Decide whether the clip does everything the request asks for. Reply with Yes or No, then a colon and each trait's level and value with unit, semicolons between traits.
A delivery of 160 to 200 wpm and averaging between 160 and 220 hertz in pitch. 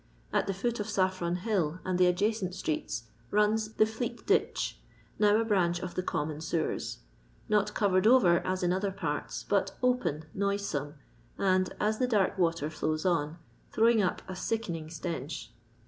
Yes: average, 165 wpm; medium, 185 Hz